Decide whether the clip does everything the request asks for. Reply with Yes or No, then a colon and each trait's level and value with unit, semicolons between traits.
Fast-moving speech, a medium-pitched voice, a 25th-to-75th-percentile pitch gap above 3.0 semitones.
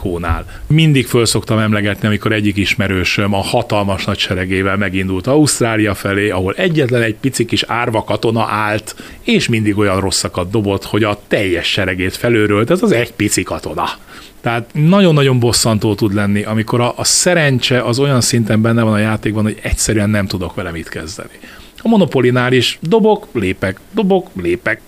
No: fast, 165 wpm; low, 110 Hz; average, 3.4 semitones